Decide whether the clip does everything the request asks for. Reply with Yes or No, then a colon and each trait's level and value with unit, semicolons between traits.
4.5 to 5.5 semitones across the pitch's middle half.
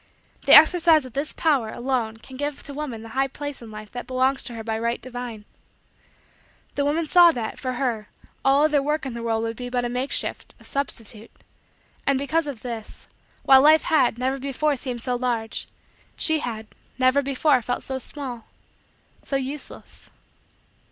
No: average, 3.3 semitones